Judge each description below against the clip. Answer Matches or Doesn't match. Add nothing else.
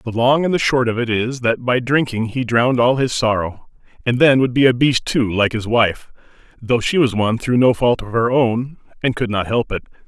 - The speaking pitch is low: Matches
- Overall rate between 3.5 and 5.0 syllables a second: Doesn't match